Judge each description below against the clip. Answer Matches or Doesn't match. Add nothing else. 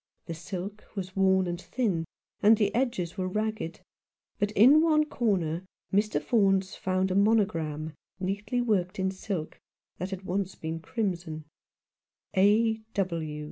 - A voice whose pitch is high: Matches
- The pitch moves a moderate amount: Matches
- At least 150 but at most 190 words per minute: Doesn't match